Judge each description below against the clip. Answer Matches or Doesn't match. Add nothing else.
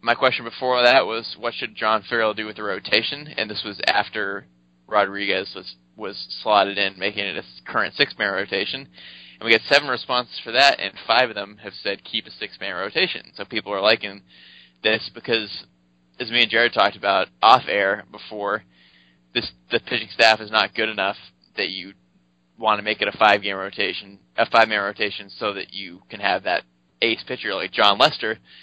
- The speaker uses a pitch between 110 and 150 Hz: Doesn't match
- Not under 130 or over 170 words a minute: Doesn't match